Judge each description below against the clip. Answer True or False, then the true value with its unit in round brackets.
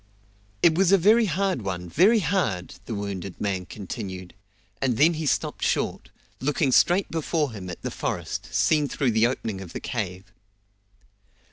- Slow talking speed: False (160 wpm)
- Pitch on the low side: True (125 Hz)